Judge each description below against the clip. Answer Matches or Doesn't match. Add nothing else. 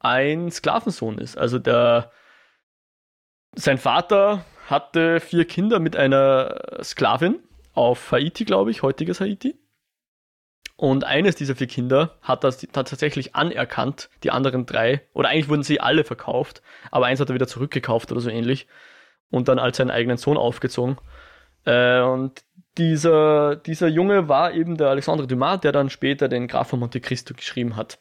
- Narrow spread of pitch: Doesn't match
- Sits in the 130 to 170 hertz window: Matches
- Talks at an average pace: Matches